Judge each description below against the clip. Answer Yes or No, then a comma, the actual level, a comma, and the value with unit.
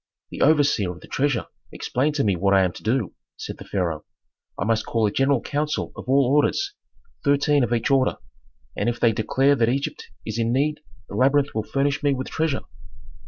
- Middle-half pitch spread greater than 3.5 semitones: Yes, average, 4.3 semitones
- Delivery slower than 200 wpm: No, fast, 205 wpm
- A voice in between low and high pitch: No, low, 130 Hz